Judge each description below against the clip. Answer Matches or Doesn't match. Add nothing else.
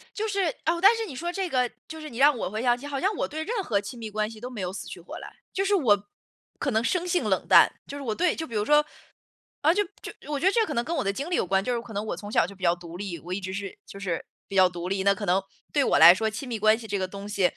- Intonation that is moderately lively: Doesn't match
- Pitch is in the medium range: Doesn't match